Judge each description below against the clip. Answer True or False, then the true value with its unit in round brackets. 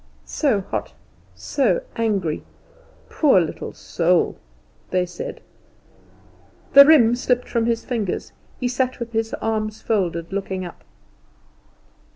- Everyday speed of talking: False (115 wpm)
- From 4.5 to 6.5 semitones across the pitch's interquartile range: True (4.8 semitones)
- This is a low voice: False (220 Hz)